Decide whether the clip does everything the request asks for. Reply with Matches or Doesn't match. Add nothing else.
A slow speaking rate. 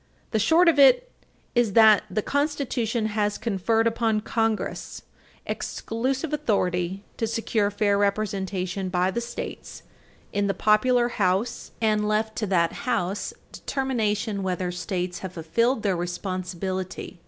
Matches